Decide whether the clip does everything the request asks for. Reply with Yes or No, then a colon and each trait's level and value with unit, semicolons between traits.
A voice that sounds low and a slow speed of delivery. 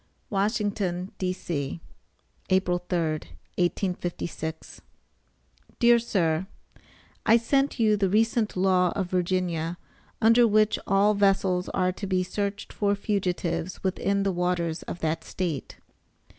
No: medium, 185 Hz; slow, 115 wpm